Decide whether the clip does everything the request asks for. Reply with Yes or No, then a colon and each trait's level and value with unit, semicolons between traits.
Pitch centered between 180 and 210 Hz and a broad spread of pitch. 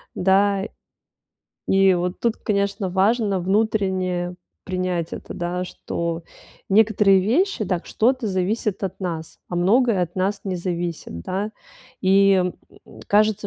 No: high, 190 Hz; narrow, 2.6 semitones